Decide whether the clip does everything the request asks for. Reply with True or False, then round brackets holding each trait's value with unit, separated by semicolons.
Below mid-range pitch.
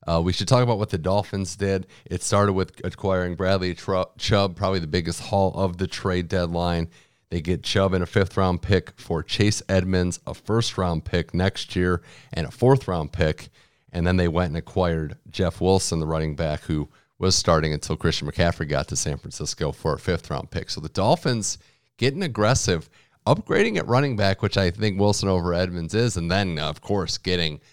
True (95 Hz)